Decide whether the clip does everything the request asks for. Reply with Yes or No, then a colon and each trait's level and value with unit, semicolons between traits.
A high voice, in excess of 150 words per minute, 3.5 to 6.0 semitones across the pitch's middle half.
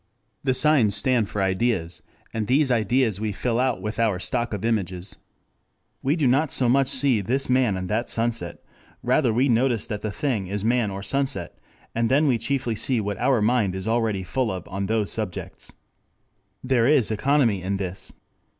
No: low, 115 Hz; average, 185 wpm; average, 4.2 semitones